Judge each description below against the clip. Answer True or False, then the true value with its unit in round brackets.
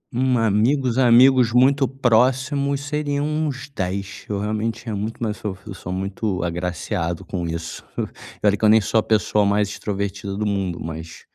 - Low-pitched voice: True (105 Hz)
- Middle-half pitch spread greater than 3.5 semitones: True (4.8 semitones)